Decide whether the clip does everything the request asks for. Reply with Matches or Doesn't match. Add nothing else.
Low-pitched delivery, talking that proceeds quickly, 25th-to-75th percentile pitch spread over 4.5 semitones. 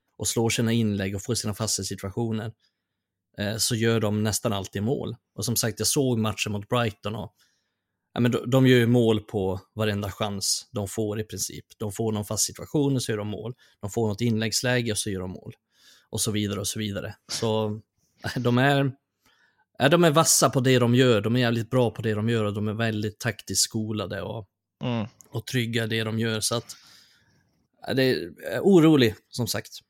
Doesn't match